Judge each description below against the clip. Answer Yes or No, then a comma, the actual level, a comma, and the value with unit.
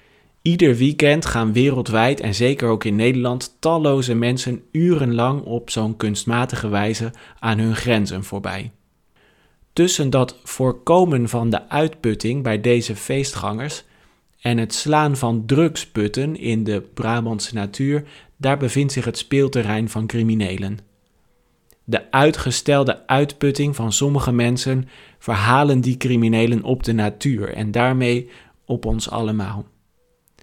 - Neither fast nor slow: No, slow, 120 wpm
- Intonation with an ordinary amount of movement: Yes, average, 3.6 semitones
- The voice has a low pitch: Yes, low, 120 Hz